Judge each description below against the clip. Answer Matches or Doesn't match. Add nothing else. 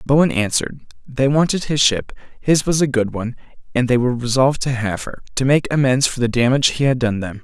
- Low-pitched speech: Matches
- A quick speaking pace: Matches